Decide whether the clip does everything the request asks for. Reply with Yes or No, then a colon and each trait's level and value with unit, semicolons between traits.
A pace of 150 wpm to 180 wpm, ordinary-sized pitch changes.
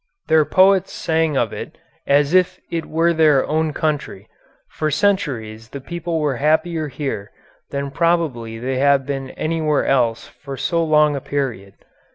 Yes: average, 155 wpm; average, 3.4 semitones